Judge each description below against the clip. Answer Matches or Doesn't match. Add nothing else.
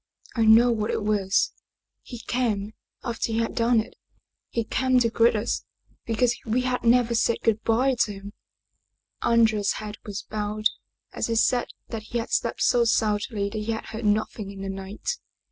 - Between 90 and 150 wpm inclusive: Doesn't match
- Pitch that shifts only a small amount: Matches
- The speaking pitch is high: Matches